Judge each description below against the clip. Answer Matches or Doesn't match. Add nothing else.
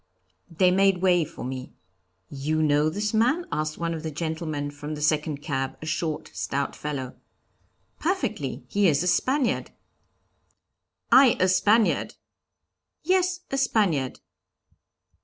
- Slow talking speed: Matches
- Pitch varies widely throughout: Matches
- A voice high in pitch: Doesn't match